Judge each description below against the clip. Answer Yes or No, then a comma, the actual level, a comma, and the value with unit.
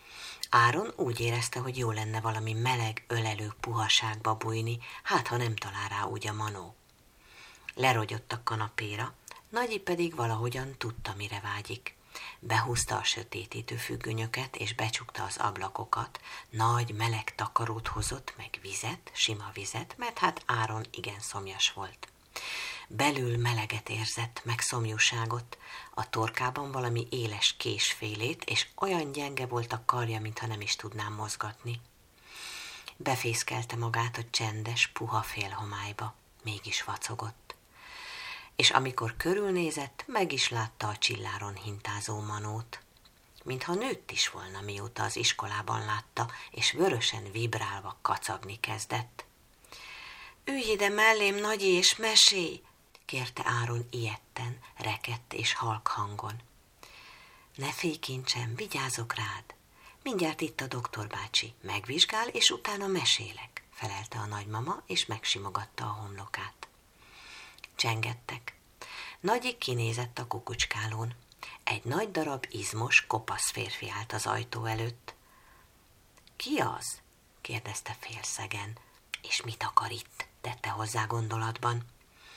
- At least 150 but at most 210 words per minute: No, average, 120 wpm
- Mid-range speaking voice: No, low, 115 Hz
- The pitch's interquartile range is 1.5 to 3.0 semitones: Yes, narrow, 2.5 semitones